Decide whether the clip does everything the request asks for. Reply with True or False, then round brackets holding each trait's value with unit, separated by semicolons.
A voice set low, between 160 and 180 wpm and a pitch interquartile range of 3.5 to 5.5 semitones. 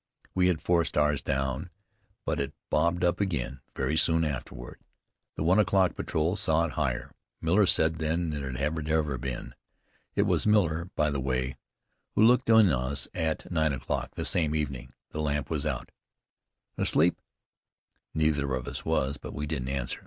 True (75 Hz; 170 wpm; 3.8 semitones)